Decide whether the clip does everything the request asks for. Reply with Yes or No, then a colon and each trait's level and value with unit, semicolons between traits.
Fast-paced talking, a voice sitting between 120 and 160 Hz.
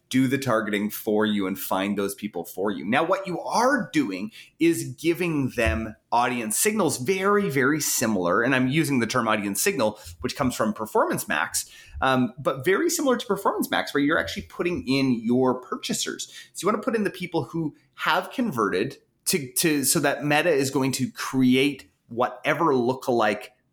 No: average, 180 wpm; low, 135 Hz